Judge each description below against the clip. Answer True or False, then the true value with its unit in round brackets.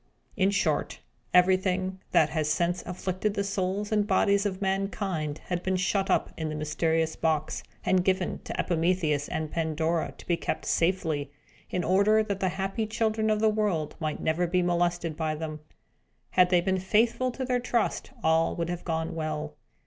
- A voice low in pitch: False (180 Hz)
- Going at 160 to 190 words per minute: True (175 wpm)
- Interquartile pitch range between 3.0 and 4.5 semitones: True (3.5 semitones)